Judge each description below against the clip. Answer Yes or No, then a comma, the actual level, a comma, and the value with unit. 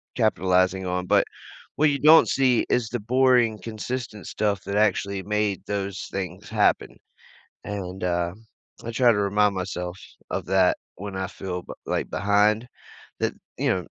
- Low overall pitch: Yes, low, 100 Hz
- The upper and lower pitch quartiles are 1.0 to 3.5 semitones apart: Yes, average, 2.9 semitones